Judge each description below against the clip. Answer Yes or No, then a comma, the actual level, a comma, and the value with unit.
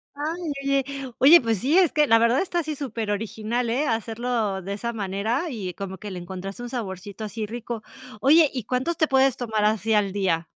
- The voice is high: Yes, high, 230 Hz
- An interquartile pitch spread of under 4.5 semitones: No, average, 4.8 semitones